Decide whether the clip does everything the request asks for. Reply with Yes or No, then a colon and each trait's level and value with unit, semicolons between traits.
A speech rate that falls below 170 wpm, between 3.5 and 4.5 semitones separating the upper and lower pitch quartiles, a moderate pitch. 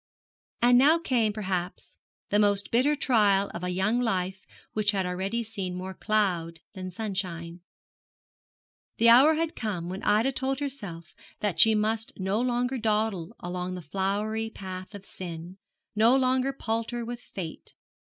No: average, 150 wpm; average, 4.1 semitones; high, 210 Hz